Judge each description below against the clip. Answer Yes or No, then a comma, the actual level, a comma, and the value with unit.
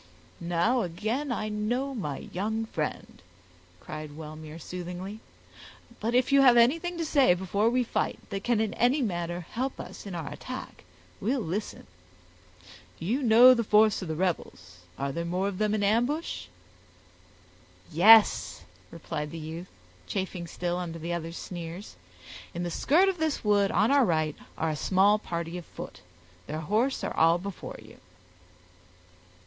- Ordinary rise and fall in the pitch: No, wide, 5.7 semitones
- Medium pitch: No, high, 195 Hz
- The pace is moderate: Yes, average, 155 wpm